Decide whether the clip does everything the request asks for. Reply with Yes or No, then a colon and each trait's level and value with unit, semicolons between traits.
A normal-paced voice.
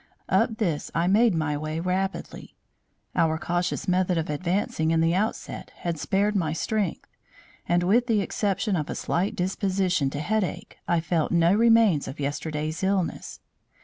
Yes: average, 155 wpm